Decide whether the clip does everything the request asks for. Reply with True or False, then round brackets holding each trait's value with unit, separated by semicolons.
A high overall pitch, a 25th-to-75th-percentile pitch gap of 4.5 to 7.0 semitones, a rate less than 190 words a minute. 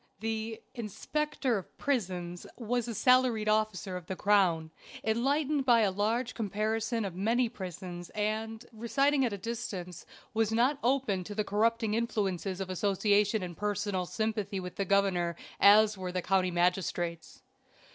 False (210 Hz; 3.5 semitones; 145 wpm)